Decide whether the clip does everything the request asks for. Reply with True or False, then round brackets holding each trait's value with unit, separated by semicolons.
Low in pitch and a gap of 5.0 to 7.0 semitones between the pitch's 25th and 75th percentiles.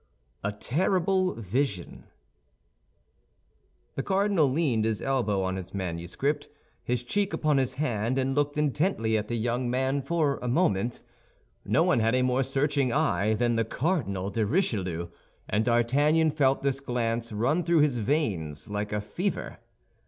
True (125 Hz; 5.4 semitones)